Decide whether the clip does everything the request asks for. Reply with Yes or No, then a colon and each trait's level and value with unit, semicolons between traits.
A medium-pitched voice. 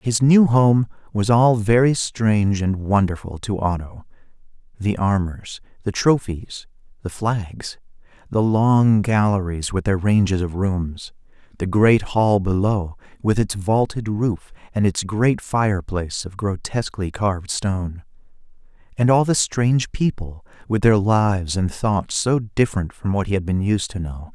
No: low, 105 Hz